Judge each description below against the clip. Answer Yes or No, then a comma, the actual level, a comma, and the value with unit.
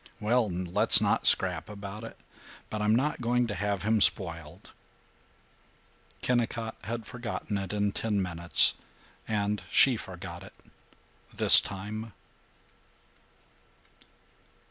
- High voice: No, low, 105 Hz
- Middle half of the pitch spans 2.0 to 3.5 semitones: Yes, average, 2.9 semitones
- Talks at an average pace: No, slow, 110 wpm